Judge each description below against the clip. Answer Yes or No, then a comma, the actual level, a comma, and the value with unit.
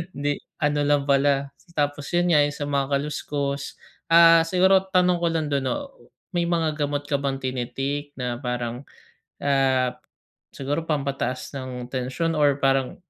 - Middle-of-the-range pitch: Yes, medium, 145 Hz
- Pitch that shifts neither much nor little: No, narrow, 2.3 semitones